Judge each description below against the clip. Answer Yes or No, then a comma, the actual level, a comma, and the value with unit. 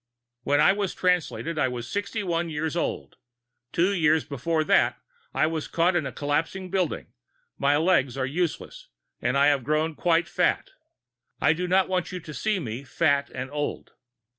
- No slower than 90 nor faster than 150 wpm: No, average, 180 wpm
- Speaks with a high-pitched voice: No, medium, 160 Hz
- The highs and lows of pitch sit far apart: No, average, 3.9 semitones